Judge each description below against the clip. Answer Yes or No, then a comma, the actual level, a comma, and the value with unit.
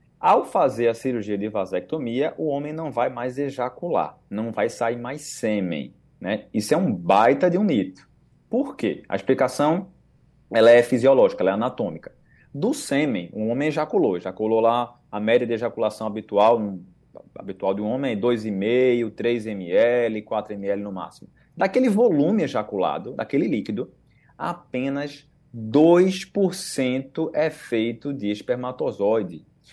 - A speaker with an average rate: Yes, average, 145 wpm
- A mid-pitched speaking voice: No, low, 120 Hz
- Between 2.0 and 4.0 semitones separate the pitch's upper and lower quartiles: No, average, 5.0 semitones